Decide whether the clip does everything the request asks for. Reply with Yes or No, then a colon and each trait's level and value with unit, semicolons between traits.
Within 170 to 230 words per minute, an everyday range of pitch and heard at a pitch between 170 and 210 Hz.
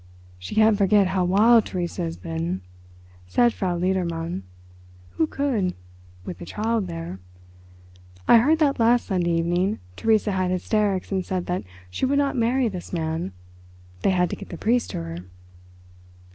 No: average, 155 wpm; average, 5.0 semitones; medium, 185 Hz